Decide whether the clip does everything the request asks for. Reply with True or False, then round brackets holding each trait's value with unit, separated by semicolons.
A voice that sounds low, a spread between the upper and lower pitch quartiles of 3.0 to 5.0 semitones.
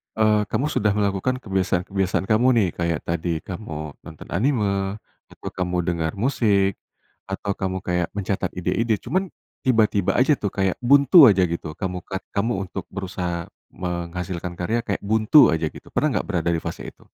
True (95 Hz; 3.5 semitones)